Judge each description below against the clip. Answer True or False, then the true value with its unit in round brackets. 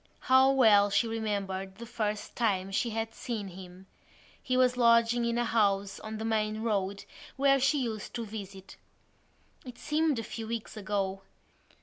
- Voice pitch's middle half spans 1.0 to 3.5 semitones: True (3.0 semitones)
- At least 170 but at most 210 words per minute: False (160 wpm)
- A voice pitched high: True (220 Hz)